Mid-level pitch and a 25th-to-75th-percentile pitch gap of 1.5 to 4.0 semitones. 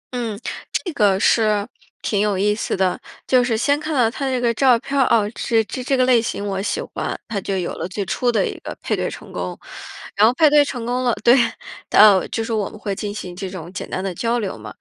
No: high, 225 Hz; average, 3.7 semitones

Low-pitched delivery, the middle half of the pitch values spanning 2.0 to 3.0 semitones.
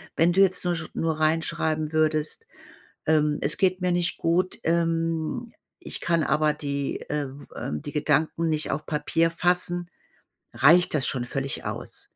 No: medium, 160 Hz; narrow, 2.4 semitones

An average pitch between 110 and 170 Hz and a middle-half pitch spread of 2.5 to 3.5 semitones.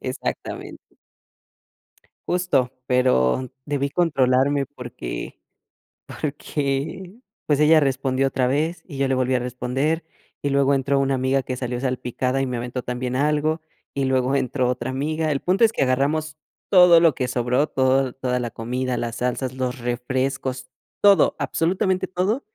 Yes: low, 135 Hz; average, 3.0 semitones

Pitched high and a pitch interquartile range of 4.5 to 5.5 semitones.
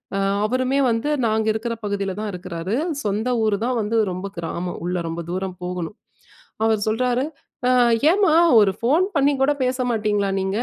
Yes: high, 215 Hz; average, 4.8 semitones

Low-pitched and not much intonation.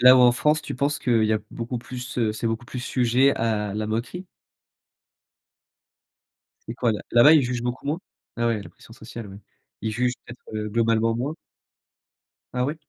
Yes: low, 120 Hz; narrow, 2.1 semitones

